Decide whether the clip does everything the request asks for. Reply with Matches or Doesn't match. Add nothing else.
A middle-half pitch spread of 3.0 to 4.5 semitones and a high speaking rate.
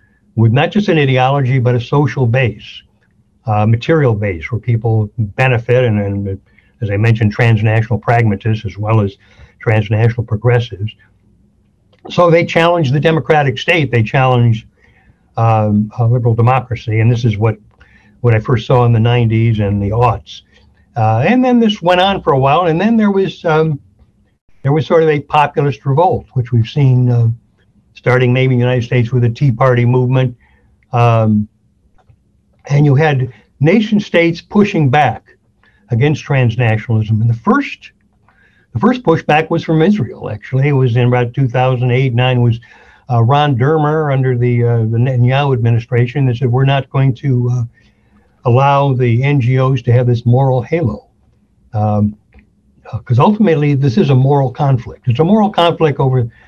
Matches